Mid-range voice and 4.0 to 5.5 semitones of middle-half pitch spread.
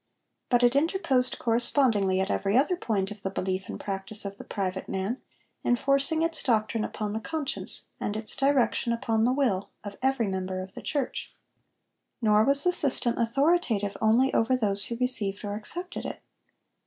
No: high, 230 Hz; average, 4.9 semitones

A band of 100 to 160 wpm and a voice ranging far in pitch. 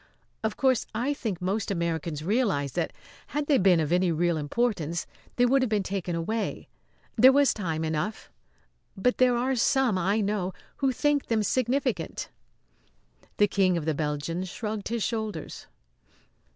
Yes: average, 155 wpm; wide, 6.2 semitones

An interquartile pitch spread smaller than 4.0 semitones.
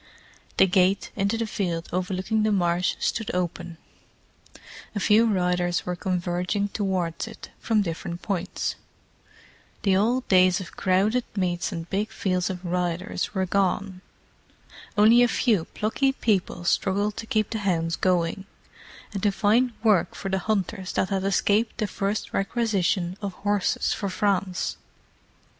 Yes: average, 2.7 semitones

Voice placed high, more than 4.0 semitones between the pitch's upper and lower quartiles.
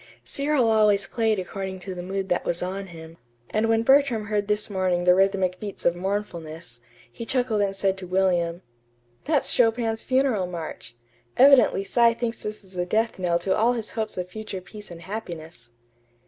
No: high, 195 Hz; average, 3.7 semitones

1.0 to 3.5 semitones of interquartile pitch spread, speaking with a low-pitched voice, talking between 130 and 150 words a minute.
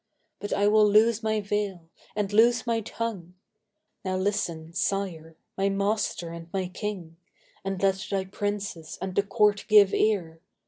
No: narrow, 2.5 semitones; high, 200 Hz; average, 145 wpm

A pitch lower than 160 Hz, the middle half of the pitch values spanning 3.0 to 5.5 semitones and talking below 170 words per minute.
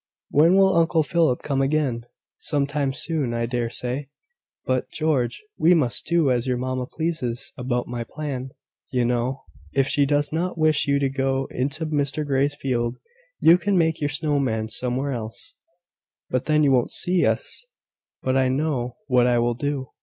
No: low, 135 Hz; average, 3.6 semitones; average, 175 wpm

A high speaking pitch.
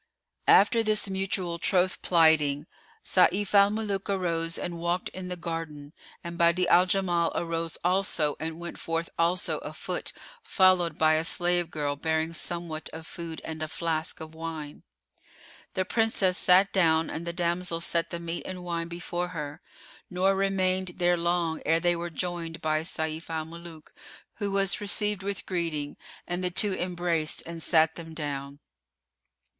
No: medium, 170 Hz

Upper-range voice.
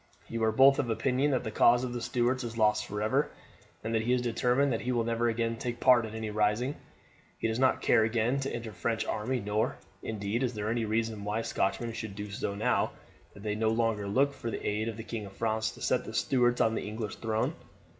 No: low, 115 Hz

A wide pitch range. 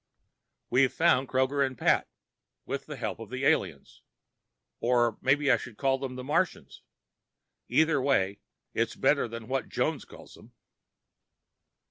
No: average, 2.7 semitones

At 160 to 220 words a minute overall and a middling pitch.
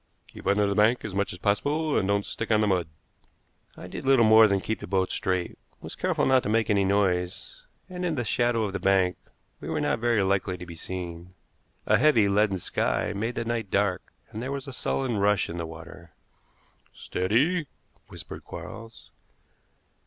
No: average, 195 wpm; low, 105 Hz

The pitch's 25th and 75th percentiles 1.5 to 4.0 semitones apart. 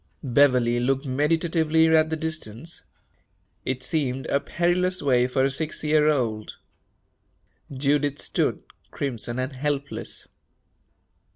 Yes: average, 3.5 semitones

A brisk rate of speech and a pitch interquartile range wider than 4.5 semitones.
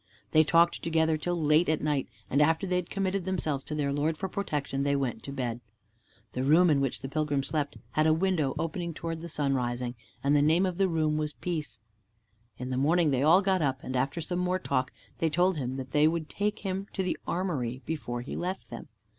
No: fast, 220 wpm; average, 4.2 semitones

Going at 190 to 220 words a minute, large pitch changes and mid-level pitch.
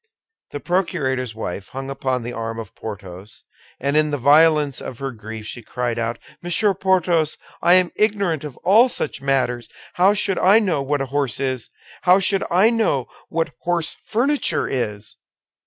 No: average, 170 wpm; wide, 6.8 semitones; medium, 145 Hz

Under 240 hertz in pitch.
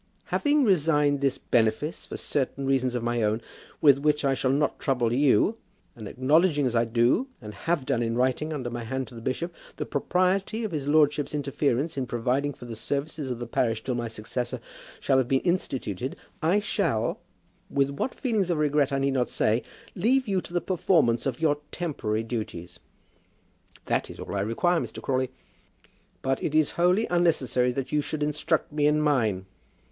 Yes: medium, 140 Hz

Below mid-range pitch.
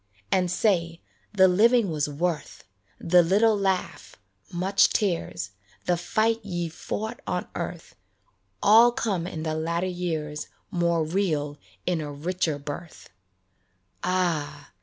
No: medium, 175 Hz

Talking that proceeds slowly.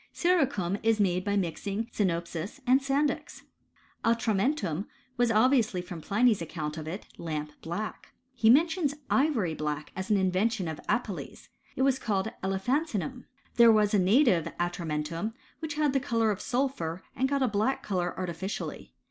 No: average, 155 wpm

